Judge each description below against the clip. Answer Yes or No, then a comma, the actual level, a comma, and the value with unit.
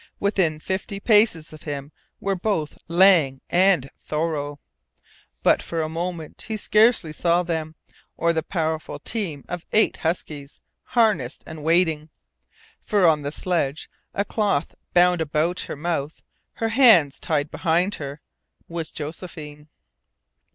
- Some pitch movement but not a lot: Yes, average, 3.6 semitones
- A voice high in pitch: No, medium, 165 Hz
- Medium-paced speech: No, slow, 130 wpm